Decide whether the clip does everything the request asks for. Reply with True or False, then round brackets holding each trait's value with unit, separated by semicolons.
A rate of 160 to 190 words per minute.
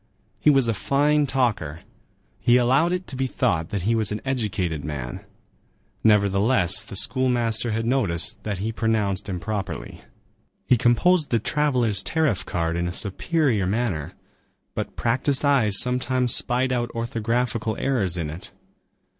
False (145 wpm)